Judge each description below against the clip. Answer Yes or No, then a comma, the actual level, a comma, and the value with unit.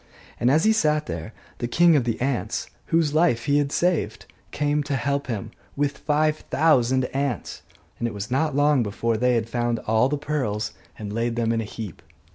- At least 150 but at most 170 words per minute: No, average, 200 wpm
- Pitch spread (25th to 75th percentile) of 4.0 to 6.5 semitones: Yes, average, 4.3 semitones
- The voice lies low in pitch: Yes, low, 130 Hz